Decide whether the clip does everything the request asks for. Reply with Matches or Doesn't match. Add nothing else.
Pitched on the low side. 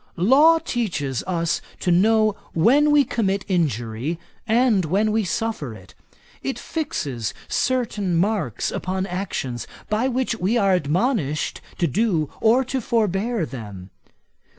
Doesn't match